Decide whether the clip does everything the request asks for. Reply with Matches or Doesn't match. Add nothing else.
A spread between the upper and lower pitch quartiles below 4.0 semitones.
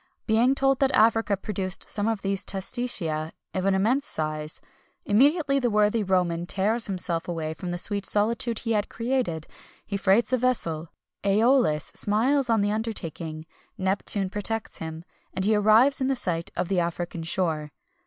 Doesn't match